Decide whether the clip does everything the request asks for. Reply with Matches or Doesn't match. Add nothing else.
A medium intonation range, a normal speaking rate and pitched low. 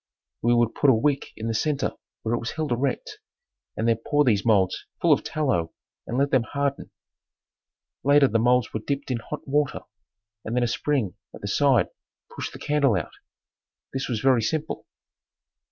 Matches